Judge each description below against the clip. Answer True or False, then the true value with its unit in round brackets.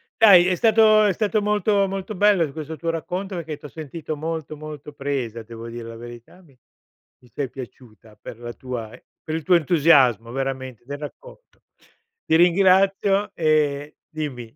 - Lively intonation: True (6.4 semitones)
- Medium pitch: True (155 Hz)